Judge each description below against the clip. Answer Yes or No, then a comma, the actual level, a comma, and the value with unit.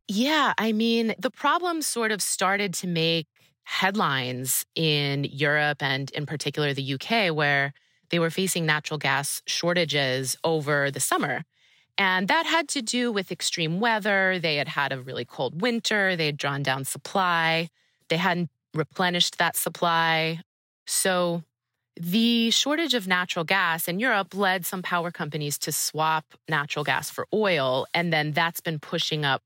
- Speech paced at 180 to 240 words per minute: No, average, 155 wpm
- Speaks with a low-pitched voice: No, medium, 165 Hz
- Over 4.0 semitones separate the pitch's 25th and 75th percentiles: Yes, average, 4.6 semitones